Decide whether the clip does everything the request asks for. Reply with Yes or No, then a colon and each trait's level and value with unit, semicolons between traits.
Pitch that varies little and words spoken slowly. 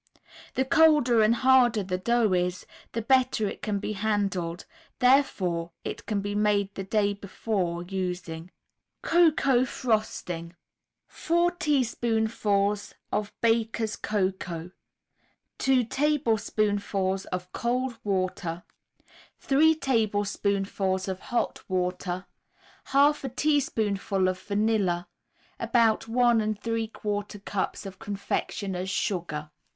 No: average, 4.0 semitones; slow, 105 wpm